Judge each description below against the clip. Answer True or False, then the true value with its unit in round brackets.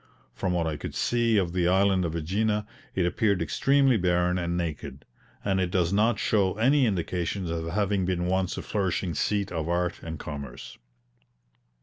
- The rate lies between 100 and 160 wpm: False (170 wpm)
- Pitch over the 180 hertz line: False (90 Hz)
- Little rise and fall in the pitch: False (3.0 semitones)